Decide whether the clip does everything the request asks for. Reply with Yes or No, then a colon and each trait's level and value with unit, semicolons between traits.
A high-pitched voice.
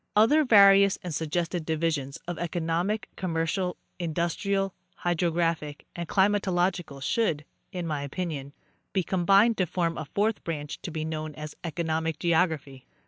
No: medium, 170 Hz